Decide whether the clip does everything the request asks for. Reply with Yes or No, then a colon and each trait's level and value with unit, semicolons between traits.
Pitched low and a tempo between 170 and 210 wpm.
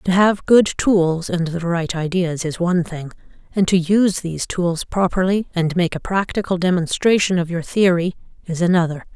No: medium, 180 Hz; average, 175 wpm